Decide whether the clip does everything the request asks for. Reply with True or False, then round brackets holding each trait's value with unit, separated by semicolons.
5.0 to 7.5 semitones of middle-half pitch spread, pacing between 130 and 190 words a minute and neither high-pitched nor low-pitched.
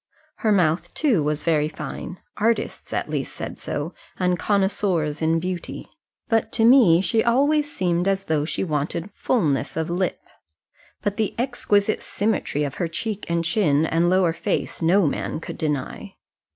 False (4.5 semitones; 160 wpm; 180 Hz)